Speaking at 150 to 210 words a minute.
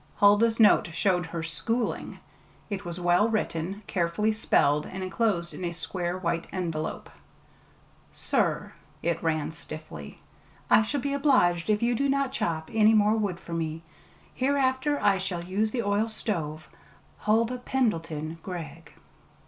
No: average, 140 wpm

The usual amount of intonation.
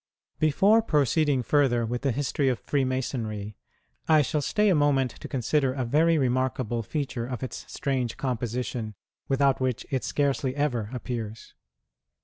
Yes: average, 3.0 semitones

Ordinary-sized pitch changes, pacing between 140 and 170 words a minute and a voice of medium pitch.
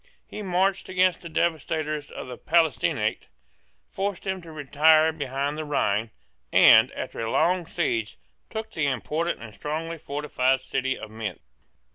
Yes: average, 4.5 semitones; average, 145 wpm; medium, 155 Hz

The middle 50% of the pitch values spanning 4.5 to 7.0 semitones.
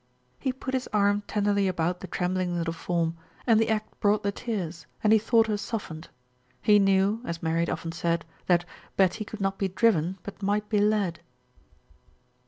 No: average, 3.6 semitones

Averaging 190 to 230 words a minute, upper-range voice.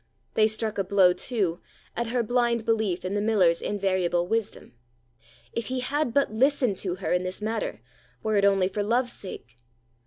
No: average, 180 wpm; high, 210 Hz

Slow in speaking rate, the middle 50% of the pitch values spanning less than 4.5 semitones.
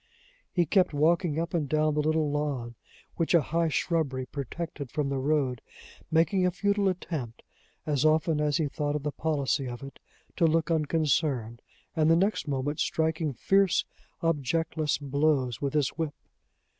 No: average, 160 wpm; average, 2.8 semitones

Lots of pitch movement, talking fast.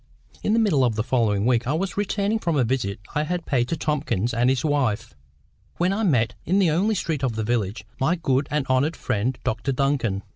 Yes: wide, 5.8 semitones; fast, 220 wpm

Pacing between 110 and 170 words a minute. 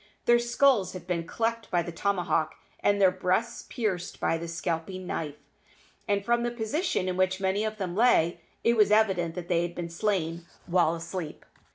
No: average, 185 wpm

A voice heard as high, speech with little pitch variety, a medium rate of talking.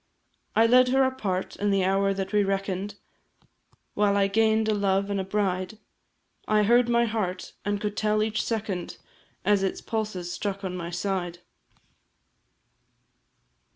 Yes: high, 200 Hz; narrow, 2.2 semitones; average, 150 wpm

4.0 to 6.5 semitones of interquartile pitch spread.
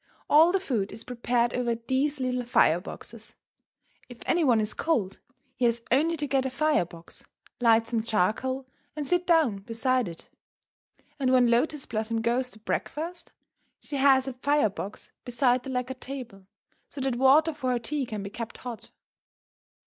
No: average, 3.4 semitones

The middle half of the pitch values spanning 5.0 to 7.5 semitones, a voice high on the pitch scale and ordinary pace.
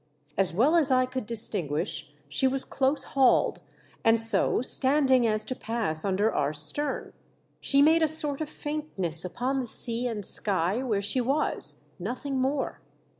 Yes: average, 5.3 semitones; high, 245 Hz; average, 160 wpm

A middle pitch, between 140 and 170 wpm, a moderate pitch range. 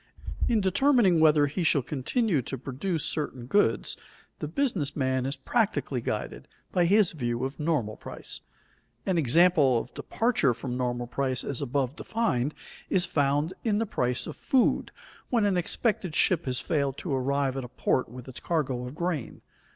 No: medium, 145 Hz; average, 165 wpm; wide, 6.0 semitones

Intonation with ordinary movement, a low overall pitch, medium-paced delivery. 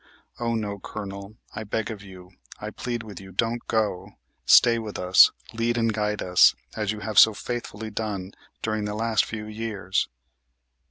No: narrow, 2.0 semitones; low, 105 Hz; average, 170 wpm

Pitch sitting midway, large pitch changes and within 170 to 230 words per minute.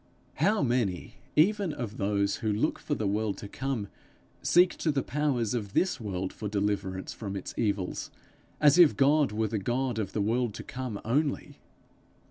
No: low, 115 Hz; wide, 5.9 semitones; average, 175 wpm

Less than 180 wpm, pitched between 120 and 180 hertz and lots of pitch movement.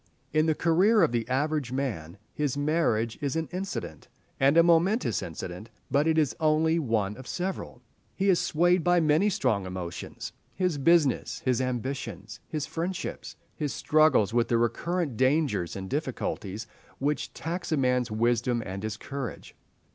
Yes: average, 155 wpm; medium, 140 Hz; wide, 5.9 semitones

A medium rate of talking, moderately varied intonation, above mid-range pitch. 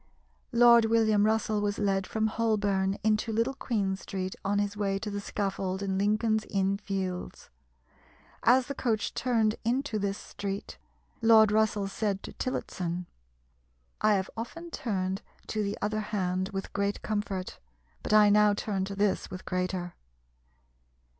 No: average, 145 wpm; narrow, 2.0 semitones; high, 205 Hz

